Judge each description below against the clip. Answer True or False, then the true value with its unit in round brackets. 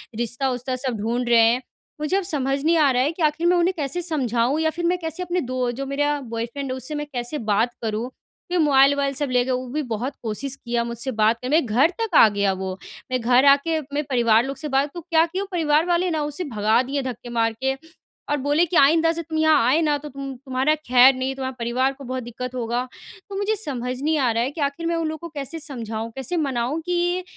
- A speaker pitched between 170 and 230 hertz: False (275 Hz)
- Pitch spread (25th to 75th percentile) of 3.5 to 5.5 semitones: True (4.3 semitones)